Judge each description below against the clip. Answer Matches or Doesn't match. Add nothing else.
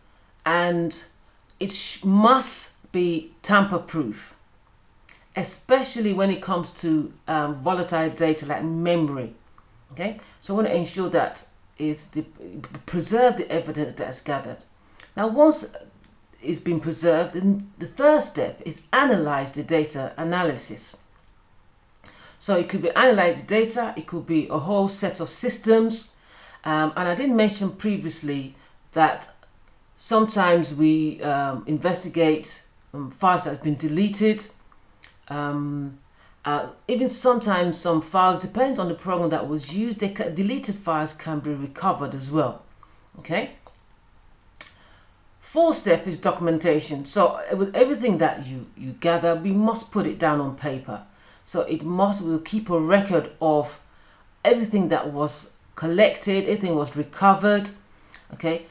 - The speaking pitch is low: Doesn't match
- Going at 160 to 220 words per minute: Doesn't match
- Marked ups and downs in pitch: Doesn't match